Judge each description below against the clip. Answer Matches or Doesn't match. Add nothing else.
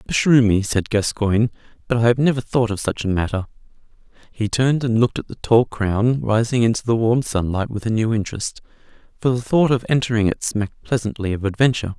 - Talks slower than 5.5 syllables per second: Doesn't match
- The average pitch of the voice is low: Matches